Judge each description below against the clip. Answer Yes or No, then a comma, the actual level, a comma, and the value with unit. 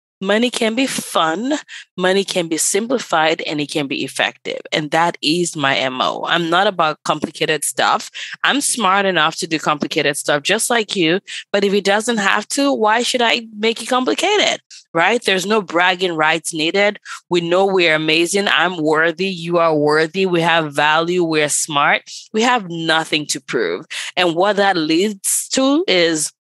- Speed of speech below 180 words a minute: Yes, average, 170 wpm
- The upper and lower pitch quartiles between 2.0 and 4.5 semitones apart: No, average, 5.3 semitones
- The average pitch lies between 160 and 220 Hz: Yes, medium, 185 Hz